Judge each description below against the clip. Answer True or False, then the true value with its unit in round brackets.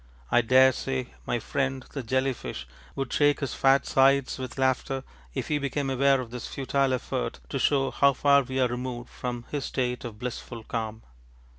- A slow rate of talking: False (180 wpm)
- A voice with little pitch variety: True (1.9 semitones)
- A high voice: False (130 Hz)